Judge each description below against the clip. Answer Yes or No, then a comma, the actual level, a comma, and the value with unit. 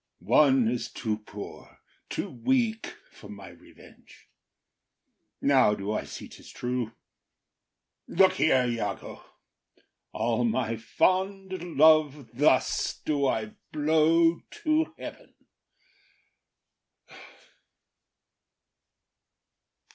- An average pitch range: No, wide, 6.4 semitones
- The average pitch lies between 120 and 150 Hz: Yes, low, 135 Hz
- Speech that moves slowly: Yes, slow, 85 wpm